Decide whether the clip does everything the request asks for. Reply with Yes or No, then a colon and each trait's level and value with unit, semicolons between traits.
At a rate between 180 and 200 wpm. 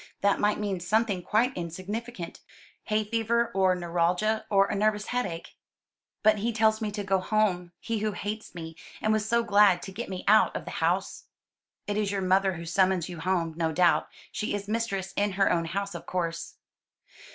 Yes: average, 190 wpm